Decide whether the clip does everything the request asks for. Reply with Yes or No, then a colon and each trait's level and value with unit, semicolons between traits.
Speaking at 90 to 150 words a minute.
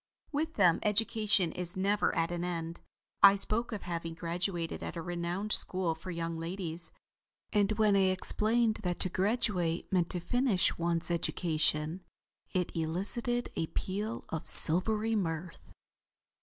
Yes: average, 140 wpm